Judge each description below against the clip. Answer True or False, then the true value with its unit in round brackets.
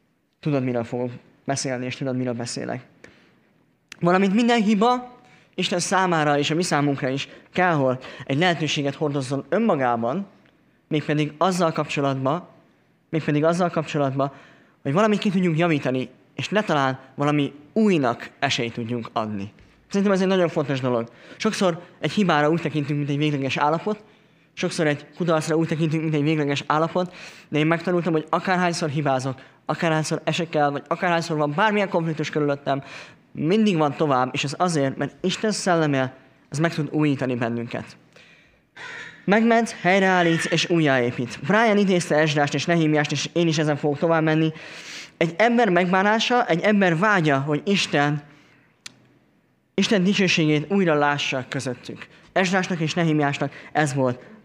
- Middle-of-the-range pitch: True (155 Hz)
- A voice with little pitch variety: False (4.2 semitones)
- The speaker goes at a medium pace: True (140 wpm)